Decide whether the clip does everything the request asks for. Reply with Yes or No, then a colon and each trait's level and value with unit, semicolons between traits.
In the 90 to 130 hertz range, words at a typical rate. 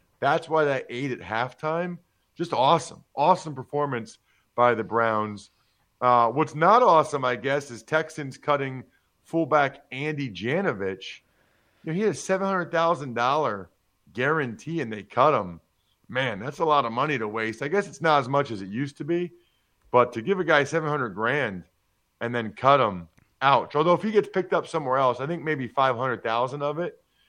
No: medium, 140 Hz; average, 190 wpm